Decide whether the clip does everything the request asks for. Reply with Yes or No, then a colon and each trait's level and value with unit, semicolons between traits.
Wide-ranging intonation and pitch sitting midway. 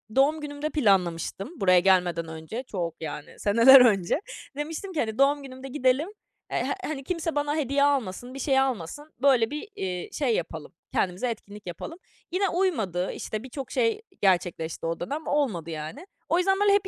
No: wide, 8.3 semitones; very high, 255 Hz